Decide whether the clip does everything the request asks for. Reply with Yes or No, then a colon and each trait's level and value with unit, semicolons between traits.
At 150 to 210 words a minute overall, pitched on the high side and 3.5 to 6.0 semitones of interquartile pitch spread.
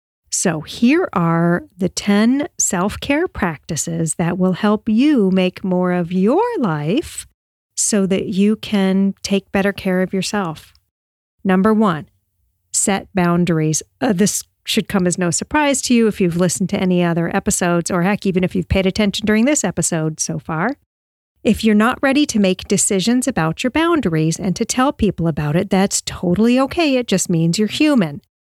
Yes: average, 175 wpm; high, 195 Hz; average, 4.1 semitones